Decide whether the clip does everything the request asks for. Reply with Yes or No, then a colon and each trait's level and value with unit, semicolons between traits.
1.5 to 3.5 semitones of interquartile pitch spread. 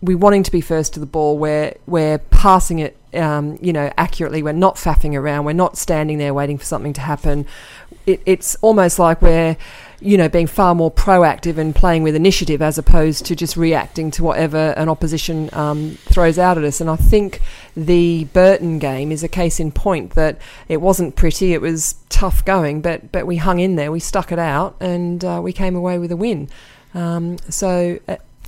Yes: average, 2.7 semitones